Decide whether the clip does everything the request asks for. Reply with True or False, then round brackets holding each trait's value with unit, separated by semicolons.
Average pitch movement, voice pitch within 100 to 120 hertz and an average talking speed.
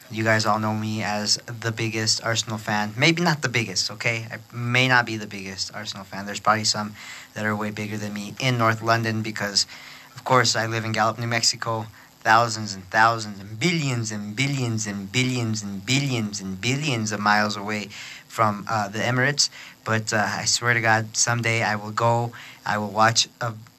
False (2.1 semitones; 110 Hz; 195 wpm)